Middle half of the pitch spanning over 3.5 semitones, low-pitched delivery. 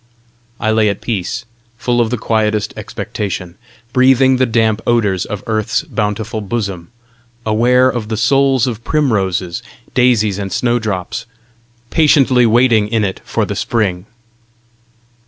No: average, 3.0 semitones; low, 110 Hz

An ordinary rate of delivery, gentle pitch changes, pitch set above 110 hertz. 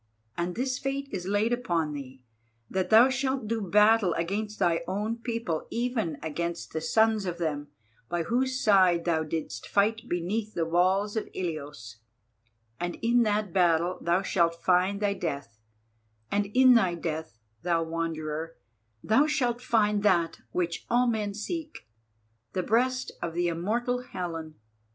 No: average, 150 wpm; average, 5.2 semitones; high, 190 Hz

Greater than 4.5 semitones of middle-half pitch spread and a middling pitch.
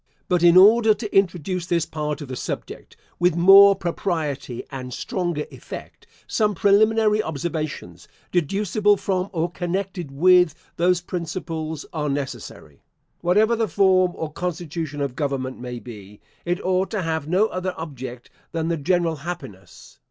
No: average, 4.2 semitones; medium, 170 Hz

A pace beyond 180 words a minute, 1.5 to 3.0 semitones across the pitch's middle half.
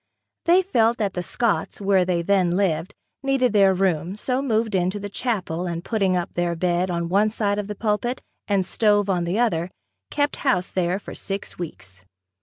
No: average, 190 wpm; average, 3.6 semitones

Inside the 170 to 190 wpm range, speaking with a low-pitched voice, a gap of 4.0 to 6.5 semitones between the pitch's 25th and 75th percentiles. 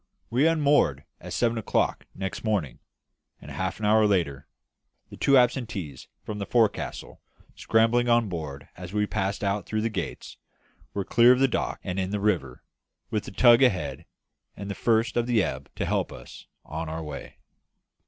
Yes: average, 175 wpm; low, 105 Hz; average, 4.6 semitones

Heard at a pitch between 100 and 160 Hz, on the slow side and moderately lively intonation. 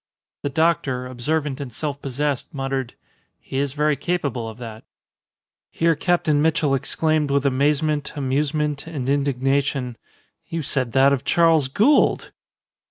No: medium, 140 Hz; slow, 130 wpm; narrow, 2.3 semitones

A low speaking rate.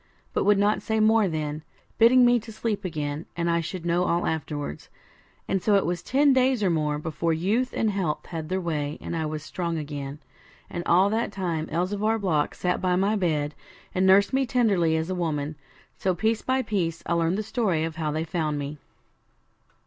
No: fast, 205 wpm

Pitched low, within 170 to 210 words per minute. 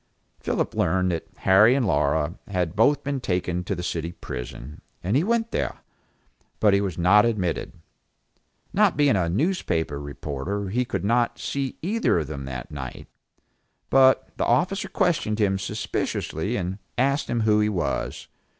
No: low, 100 Hz; average, 160 wpm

